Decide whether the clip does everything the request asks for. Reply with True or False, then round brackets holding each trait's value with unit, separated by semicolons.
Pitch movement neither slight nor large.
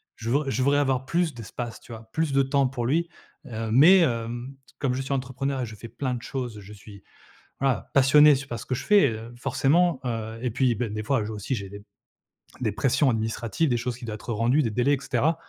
True (3.3 semitones)